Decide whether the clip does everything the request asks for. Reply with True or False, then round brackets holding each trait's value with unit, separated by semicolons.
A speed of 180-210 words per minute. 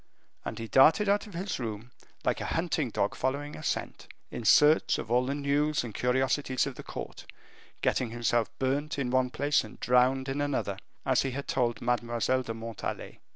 True (190 wpm)